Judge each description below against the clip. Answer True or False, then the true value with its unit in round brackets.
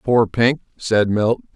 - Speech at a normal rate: True (155 wpm)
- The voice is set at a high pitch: False (115 Hz)